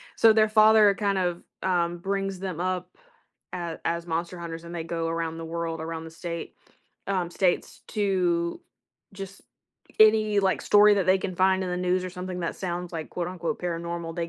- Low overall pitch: No, medium, 180 Hz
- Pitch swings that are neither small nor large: No, narrow, 2.3 semitones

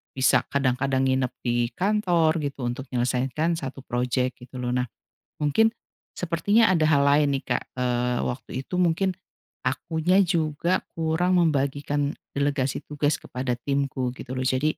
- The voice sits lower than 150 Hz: Yes, medium, 140 Hz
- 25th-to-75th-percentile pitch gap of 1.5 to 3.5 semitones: No, average, 4.0 semitones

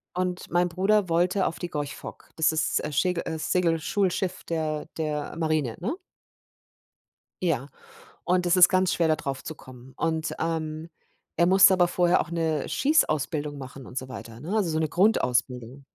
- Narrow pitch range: No, average, 3.3 semitones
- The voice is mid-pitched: Yes, medium, 160 Hz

